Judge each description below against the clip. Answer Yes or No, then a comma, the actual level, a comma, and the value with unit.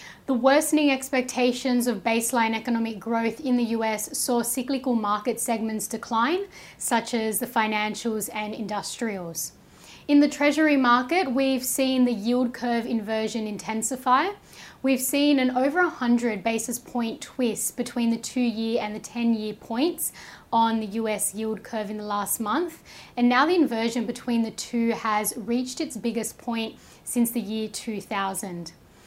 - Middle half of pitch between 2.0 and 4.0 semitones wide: Yes, narrow, 2.5 semitones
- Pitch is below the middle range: No, high, 235 Hz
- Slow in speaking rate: No, average, 155 wpm